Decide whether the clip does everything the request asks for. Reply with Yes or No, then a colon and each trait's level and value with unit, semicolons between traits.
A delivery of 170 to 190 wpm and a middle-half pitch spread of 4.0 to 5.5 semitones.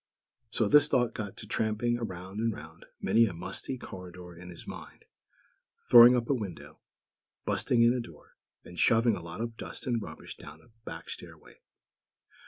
Yes: average, 175 wpm; average, 4.9 semitones